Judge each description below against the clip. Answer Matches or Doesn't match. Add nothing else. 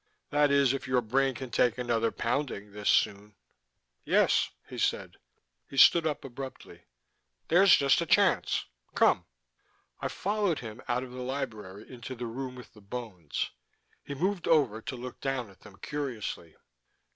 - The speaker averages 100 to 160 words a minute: Matches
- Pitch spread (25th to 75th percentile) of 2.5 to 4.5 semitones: Matches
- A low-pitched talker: Matches